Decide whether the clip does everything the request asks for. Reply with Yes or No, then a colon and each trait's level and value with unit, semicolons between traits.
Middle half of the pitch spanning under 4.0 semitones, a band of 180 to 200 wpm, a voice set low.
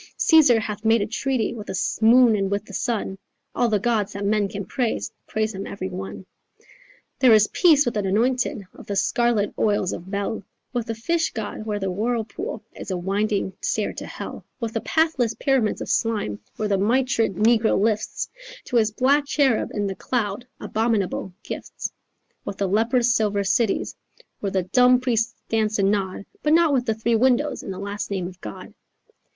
No: average, 3.2 semitones; average, 190 wpm; high, 220 Hz